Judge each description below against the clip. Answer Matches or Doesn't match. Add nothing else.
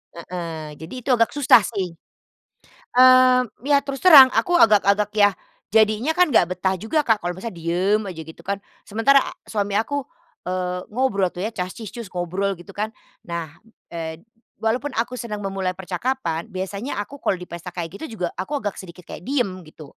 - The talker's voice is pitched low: Doesn't match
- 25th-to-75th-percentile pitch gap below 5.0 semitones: Doesn't match